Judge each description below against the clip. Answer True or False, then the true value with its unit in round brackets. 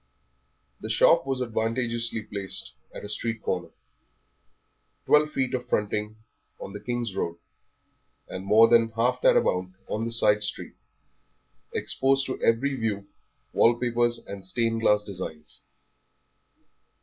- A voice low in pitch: True (115 Hz)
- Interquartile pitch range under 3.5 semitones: True (2.8 semitones)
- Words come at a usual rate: False (130 wpm)